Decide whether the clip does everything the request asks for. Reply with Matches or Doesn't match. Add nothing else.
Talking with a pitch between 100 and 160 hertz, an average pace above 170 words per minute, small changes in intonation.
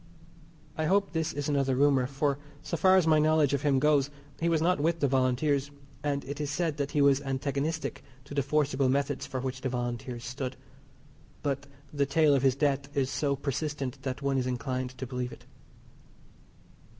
Matches